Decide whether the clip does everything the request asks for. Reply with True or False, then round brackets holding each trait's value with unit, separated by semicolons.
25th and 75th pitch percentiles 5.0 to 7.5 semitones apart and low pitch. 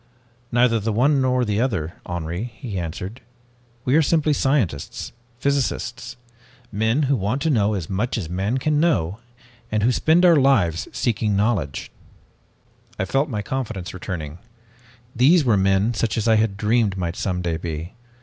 True (5.4 semitones; 110 Hz)